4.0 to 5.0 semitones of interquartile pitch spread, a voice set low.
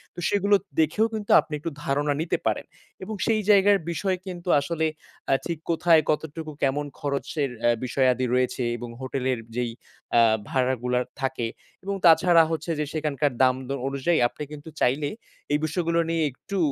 No: average, 4.3 semitones; medium, 150 Hz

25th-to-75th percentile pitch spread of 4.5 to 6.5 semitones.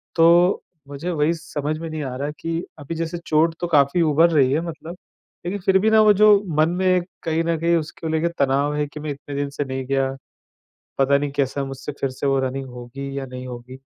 No: average, 3.5 semitones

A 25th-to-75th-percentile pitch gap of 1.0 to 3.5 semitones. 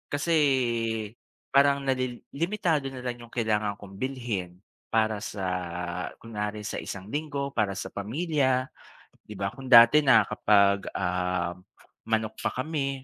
No: wide, 5.4 semitones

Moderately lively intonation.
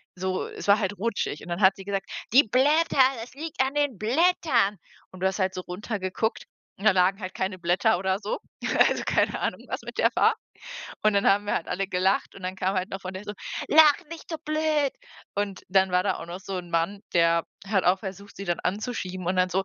Yes: average, 3.1 semitones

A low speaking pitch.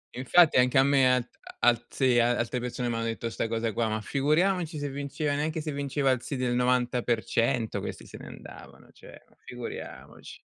Yes: low, 125 Hz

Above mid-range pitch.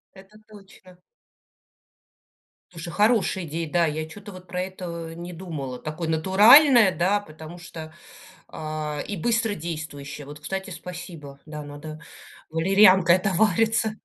No: medium, 175 Hz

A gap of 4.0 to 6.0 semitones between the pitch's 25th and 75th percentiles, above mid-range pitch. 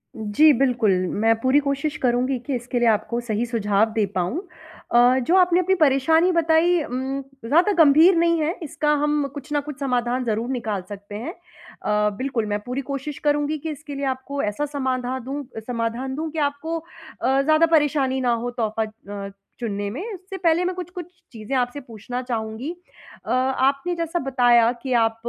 Yes: average, 4.7 semitones; very high, 265 Hz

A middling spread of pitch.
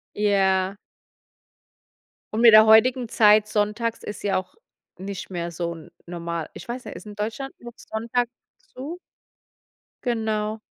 Yes: average, 3.3 semitones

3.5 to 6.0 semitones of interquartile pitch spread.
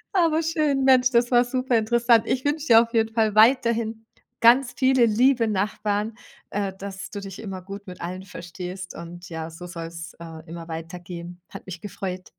Yes: average, 5.3 semitones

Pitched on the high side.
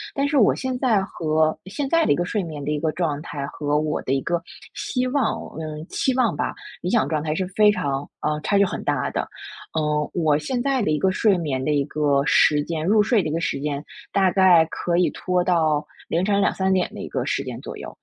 No: medium, 170 Hz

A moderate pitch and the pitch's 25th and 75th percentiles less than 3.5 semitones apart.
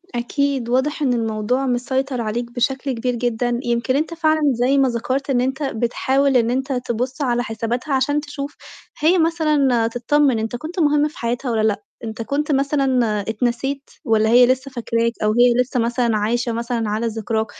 No: high, 245 Hz; average, 2.9 semitones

